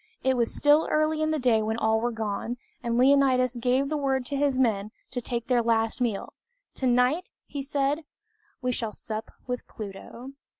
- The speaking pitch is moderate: No, very high, 250 Hz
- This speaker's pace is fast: No, average, 180 wpm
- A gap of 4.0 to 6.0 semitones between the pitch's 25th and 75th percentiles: No, average, 3.3 semitones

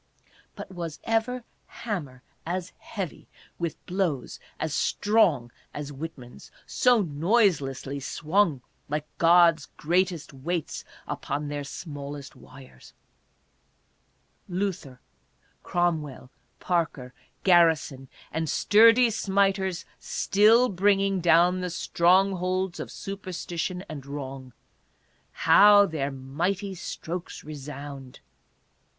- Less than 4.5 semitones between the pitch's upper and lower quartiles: No, average, 5.1 semitones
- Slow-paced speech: Yes, slow, 95 wpm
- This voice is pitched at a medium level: Yes, medium, 170 Hz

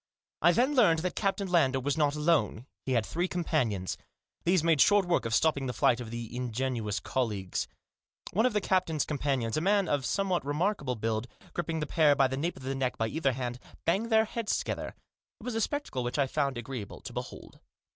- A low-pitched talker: No, medium, 145 Hz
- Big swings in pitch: Yes, wide, 6.1 semitones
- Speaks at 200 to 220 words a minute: Yes, fast, 205 wpm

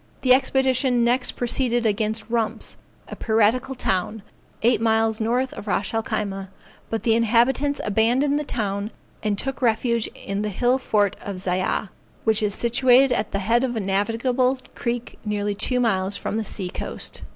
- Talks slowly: No, average, 165 wpm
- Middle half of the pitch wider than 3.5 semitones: No, average, 3.1 semitones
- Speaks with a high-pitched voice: Yes, high, 225 Hz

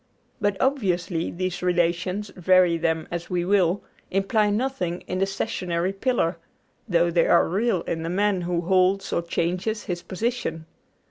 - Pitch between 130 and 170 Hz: No, medium, 180 Hz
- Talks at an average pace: Yes, average, 150 wpm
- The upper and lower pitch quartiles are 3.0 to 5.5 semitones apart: No, narrow, 2.5 semitones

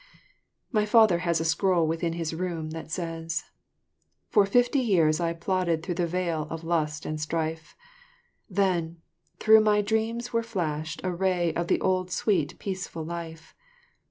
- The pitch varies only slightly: No, average, 3.1 semitones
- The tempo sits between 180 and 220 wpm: No, average, 155 wpm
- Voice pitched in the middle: Yes, medium, 170 Hz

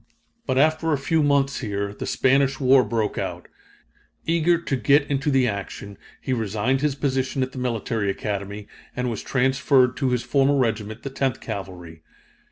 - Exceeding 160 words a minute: Yes, average, 170 wpm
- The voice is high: No, low, 130 Hz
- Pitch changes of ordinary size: Yes, average, 4.4 semitones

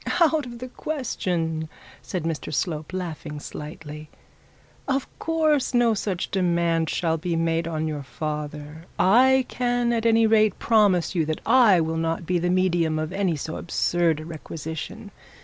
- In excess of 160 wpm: No, average, 155 wpm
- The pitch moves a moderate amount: No, wide, 5.9 semitones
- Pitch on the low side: No, medium, 170 Hz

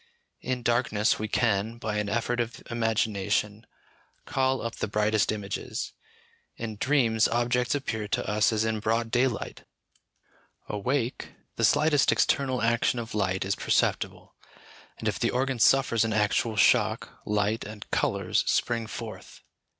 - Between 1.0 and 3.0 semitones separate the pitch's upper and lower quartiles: Yes, narrow, 2.4 semitones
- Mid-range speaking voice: No, low, 115 Hz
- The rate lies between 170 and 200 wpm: No, average, 140 wpm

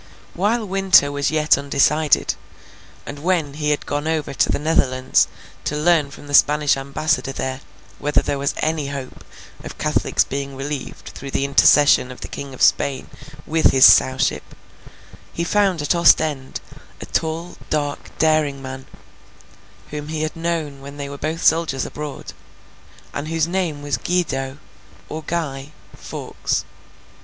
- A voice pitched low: No, medium, 145 Hz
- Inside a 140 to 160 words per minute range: Yes, average, 145 wpm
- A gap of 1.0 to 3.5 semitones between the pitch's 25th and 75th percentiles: Yes, narrow, 2.4 semitones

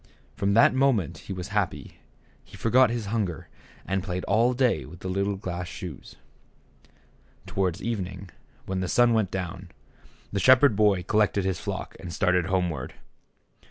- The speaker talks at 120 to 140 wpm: No, average, 160 wpm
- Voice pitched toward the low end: Yes, very low, 95 Hz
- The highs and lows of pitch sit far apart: No, average, 3.4 semitones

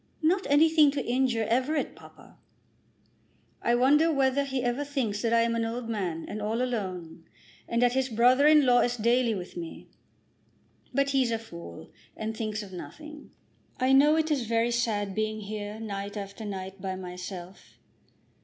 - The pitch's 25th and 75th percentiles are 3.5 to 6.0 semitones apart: Yes, average, 4.4 semitones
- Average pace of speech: Yes, average, 170 wpm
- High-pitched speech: Yes, high, 230 Hz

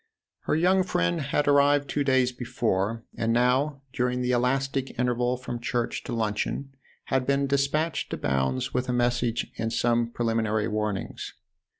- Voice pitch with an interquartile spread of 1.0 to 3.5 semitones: Yes, average, 2.9 semitones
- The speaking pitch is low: Yes, low, 125 Hz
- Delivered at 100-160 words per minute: Yes, average, 155 wpm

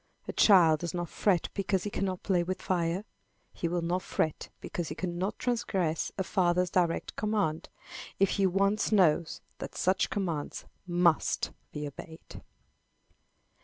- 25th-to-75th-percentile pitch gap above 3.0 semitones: No, narrow, 2.5 semitones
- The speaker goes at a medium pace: Yes, average, 145 wpm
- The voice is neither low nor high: Yes, medium, 180 Hz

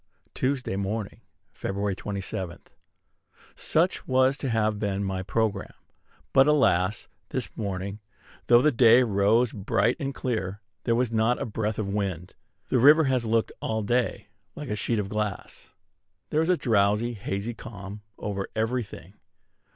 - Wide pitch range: No, average, 3.7 semitones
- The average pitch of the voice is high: No, low, 110 Hz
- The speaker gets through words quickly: No, average, 150 wpm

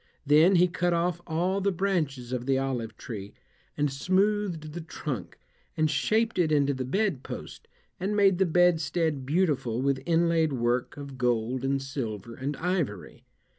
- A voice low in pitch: No, medium, 155 Hz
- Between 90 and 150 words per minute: No, average, 160 wpm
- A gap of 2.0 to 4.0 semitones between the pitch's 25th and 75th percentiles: No, average, 5.2 semitones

